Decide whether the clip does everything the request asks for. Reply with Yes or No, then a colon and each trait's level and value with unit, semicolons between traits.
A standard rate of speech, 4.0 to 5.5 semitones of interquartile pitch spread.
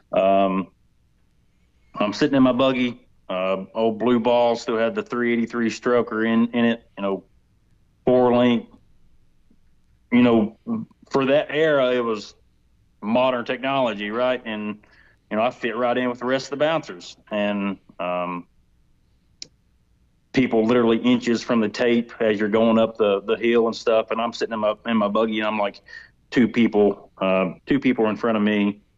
No: average, 170 wpm; average, 3.0 semitones